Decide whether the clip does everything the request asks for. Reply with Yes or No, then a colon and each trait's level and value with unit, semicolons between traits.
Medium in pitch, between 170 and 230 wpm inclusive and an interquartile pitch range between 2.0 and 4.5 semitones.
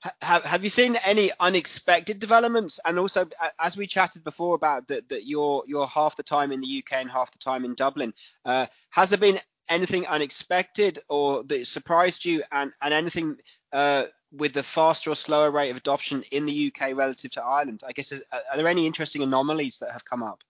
Yes: medium, 155 Hz; average, 200 wpm; average, 4.1 semitones